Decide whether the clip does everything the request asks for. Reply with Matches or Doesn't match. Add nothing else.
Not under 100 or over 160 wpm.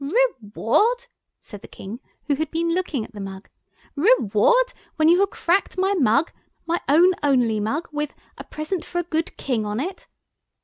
Doesn't match